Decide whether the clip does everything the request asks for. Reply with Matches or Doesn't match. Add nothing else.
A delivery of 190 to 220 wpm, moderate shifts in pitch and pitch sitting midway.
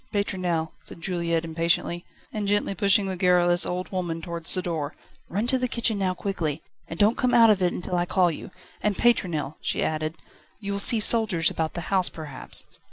Matches